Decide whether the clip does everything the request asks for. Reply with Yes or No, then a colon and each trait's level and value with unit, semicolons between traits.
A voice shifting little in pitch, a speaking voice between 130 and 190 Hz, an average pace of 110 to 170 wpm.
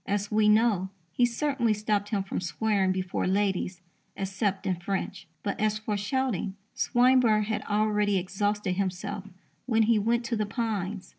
No: narrow, 2.3 semitones; high, 205 Hz; average, 155 wpm